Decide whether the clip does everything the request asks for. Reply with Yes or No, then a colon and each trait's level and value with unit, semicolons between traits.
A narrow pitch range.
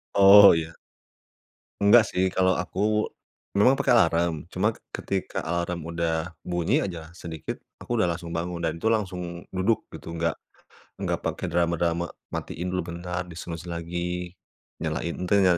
Yes: narrow, 1.9 semitones